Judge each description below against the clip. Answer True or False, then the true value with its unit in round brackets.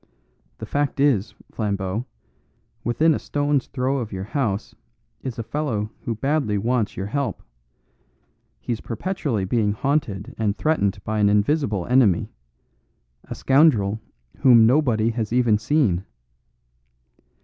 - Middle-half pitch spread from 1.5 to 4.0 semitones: False (5.2 semitones)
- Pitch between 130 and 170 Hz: False (115 Hz)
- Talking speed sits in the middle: False (125 wpm)